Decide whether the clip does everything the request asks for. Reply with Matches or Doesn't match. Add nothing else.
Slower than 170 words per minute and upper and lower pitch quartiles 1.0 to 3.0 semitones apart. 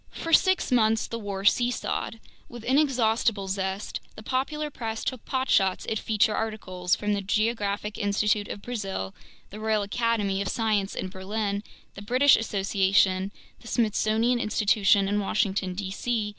Matches